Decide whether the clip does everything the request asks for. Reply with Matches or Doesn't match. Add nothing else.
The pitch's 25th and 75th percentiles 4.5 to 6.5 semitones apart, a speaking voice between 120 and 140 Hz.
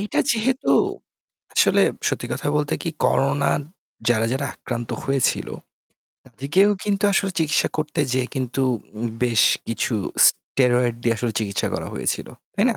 Matches